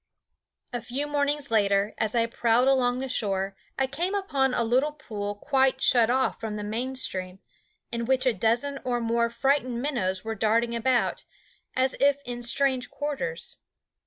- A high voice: Yes, high, 245 Hz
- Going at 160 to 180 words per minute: Yes, average, 165 wpm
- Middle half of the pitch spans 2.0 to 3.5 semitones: Yes, average, 3.2 semitones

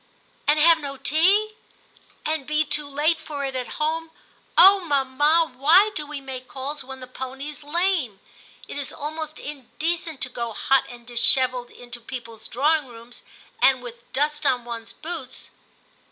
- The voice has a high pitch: Yes, very high, 285 Hz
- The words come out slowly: No, average, 165 wpm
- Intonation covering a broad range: No, average, 3.6 semitones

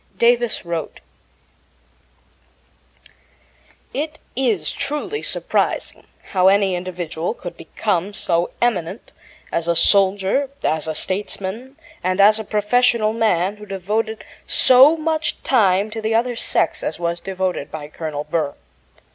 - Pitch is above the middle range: Yes, high, 200 Hz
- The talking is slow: Yes, slow, 120 wpm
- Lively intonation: No, average, 5.0 semitones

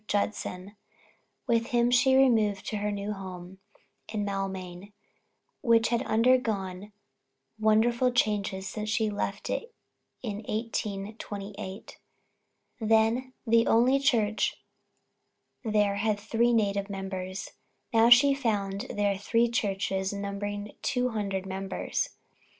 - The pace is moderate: No, slow, 110 wpm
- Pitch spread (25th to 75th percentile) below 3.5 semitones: Yes, average, 2.7 semitones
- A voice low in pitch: No, high, 210 Hz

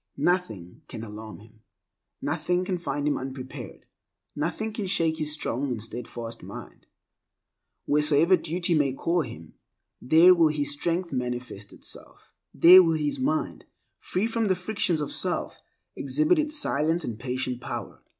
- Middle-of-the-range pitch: Yes, medium, 155 Hz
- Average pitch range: No, wide, 6.1 semitones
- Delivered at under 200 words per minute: Yes, average, 145 wpm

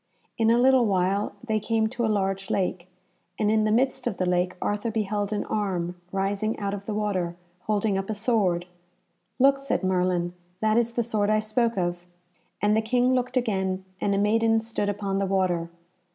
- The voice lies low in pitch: No, high, 210 Hz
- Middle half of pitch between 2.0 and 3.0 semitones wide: Yes, average, 2.7 semitones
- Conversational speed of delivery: Yes, average, 195 wpm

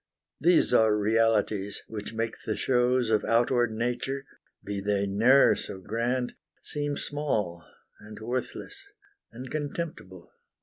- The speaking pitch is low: Yes, low, 115 Hz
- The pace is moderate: No, slow, 120 wpm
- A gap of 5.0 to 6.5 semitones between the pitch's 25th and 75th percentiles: No, average, 3.8 semitones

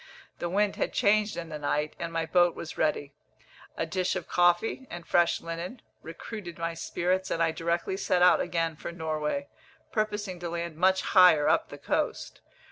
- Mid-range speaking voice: Yes, medium, 175 Hz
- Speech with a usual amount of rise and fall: No, narrow, 2.2 semitones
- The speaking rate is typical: Yes, average, 180 wpm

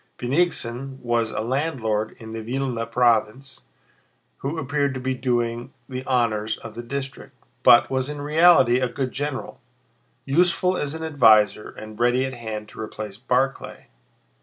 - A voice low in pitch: Yes, low, 125 Hz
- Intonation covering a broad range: No, average, 3.1 semitones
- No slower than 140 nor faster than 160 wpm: Yes, average, 150 wpm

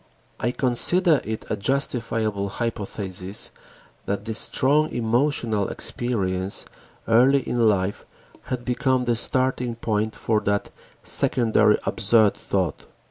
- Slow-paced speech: Yes, slow, 110 wpm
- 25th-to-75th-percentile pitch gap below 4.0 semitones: Yes, average, 3.6 semitones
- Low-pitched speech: Yes, low, 115 Hz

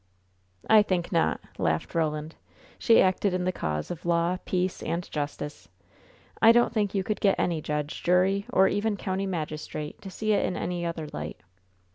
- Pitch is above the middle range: No, medium, 180 Hz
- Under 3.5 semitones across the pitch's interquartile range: No, average, 4.1 semitones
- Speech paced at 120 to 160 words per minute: No, average, 175 wpm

